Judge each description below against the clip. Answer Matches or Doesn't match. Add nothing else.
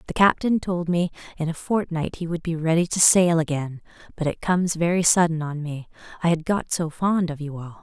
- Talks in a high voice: Doesn't match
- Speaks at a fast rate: Matches